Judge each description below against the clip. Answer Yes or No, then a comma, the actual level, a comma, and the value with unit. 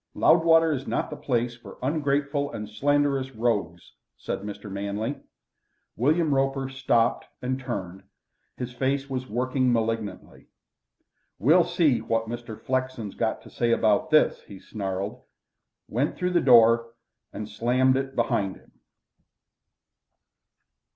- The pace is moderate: No, slow, 125 wpm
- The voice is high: No, low, 125 Hz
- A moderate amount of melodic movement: Yes, average, 3.8 semitones